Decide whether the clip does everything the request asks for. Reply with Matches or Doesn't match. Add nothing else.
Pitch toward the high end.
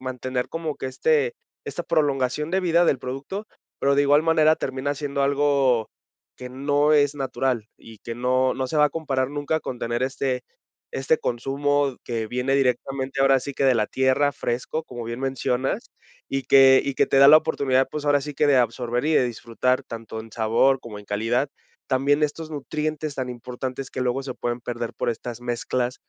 Doesn't match